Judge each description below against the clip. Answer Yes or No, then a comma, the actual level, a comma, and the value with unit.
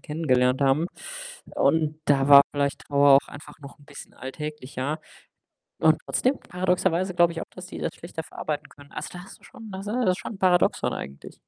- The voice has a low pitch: No, medium, 155 Hz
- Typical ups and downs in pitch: Yes, average, 4.2 semitones